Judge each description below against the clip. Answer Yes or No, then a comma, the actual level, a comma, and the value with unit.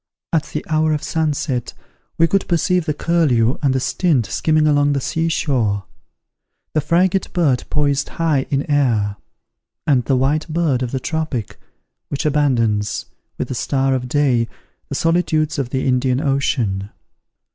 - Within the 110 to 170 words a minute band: Yes, average, 150 wpm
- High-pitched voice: No, medium, 145 Hz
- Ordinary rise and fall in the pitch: Yes, average, 3.7 semitones